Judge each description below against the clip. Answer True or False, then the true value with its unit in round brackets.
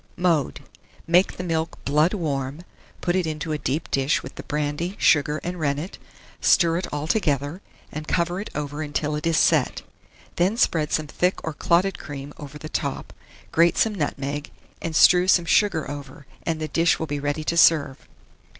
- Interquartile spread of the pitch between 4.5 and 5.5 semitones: False (2.9 semitones)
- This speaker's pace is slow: False (175 wpm)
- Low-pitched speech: False (155 Hz)